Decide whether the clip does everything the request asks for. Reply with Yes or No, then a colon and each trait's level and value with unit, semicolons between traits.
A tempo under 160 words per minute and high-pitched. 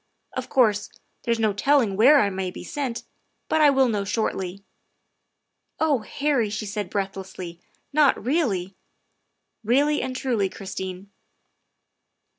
Yes: average, 150 wpm; high, 215 Hz